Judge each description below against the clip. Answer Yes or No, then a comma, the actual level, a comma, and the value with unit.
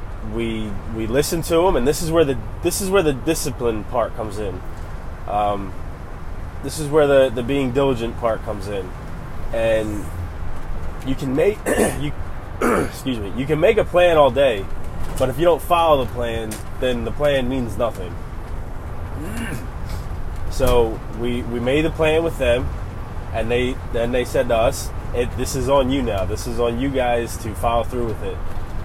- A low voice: Yes, low, 115 Hz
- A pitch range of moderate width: No, wide, 5.9 semitones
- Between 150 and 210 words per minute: Yes, average, 175 wpm